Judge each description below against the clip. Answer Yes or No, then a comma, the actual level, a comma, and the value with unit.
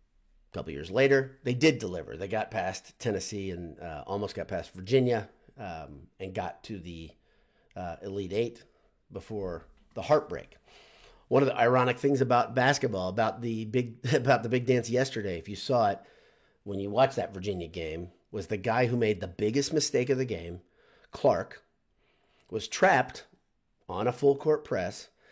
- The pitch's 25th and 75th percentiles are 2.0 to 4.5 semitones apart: No, wide, 5.4 semitones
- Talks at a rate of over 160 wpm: Yes, average, 170 wpm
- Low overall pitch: Yes, low, 115 Hz